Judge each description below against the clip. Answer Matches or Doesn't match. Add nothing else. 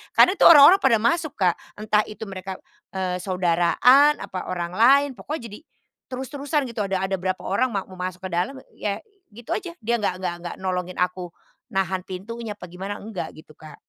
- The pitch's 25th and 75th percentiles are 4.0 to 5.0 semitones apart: Matches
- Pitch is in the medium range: Doesn't match